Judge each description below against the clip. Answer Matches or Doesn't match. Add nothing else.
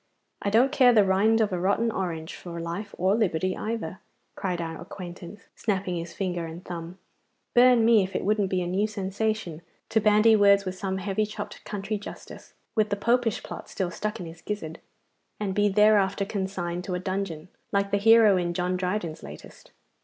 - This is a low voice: Doesn't match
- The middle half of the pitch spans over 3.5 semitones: Doesn't match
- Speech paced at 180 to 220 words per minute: Matches